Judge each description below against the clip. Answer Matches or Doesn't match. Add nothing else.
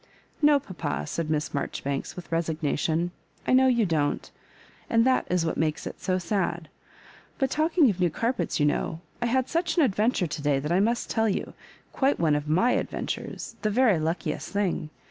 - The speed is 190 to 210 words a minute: Matches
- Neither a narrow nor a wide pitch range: Doesn't match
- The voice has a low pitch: Doesn't match